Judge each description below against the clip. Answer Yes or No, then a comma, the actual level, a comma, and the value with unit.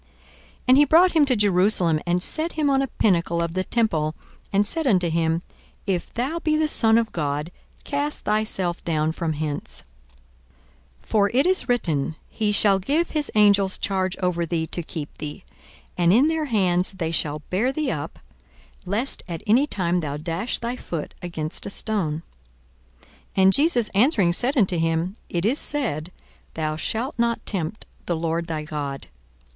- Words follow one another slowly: No, average, 175 wpm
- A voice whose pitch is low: No, high, 190 Hz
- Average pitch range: No, wide, 6.5 semitones